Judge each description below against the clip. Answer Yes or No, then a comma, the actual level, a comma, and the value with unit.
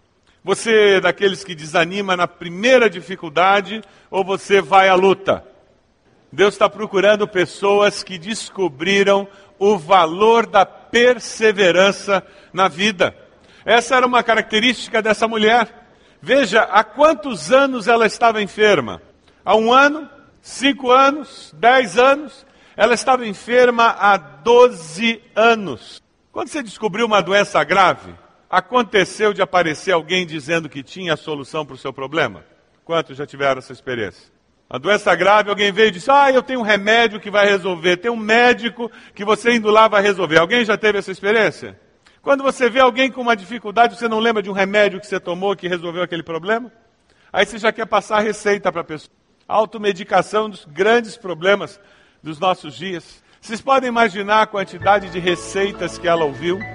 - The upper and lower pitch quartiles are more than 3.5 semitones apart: Yes, average, 3.9 semitones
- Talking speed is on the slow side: No, average, 160 wpm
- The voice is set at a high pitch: Yes, high, 205 Hz